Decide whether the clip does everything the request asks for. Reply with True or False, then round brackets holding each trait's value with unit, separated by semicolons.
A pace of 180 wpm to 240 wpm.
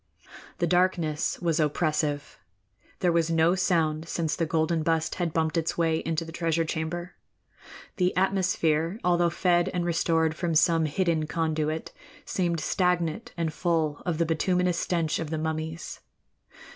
False (145 wpm)